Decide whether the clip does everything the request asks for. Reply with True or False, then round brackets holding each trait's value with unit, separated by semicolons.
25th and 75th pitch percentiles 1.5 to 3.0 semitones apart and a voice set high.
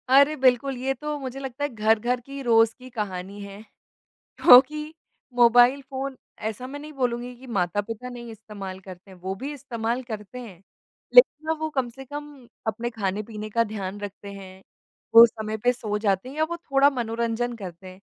False (4.2 semitones; 235 Hz)